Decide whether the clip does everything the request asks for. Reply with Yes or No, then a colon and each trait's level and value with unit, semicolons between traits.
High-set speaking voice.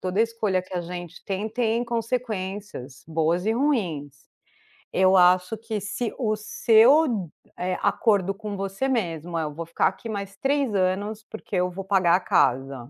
Yes: high, 195 Hz